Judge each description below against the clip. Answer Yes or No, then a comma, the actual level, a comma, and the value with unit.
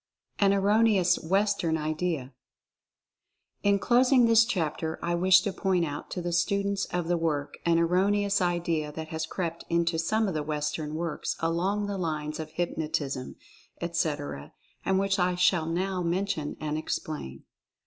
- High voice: No, medium, 170 Hz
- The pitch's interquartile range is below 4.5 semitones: Yes, average, 3.7 semitones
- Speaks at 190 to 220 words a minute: No, average, 150 wpm